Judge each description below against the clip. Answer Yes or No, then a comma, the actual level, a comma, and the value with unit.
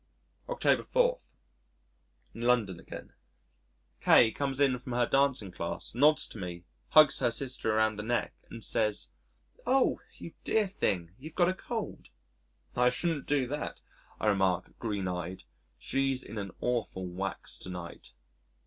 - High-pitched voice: No, low, 120 Hz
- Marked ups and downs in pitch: Yes, wide, 6.3 semitones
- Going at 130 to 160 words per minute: Yes, average, 150 wpm